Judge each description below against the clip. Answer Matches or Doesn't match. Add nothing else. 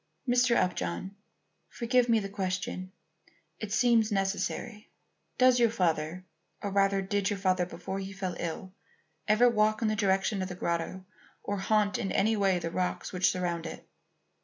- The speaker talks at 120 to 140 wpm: Doesn't match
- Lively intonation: Doesn't match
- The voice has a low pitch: Doesn't match